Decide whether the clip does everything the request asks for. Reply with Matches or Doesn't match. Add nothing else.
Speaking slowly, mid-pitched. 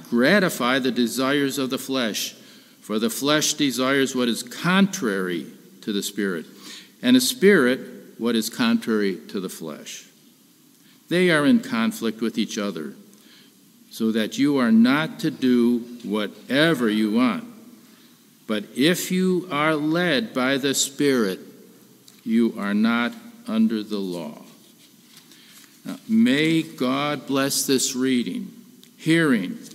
Matches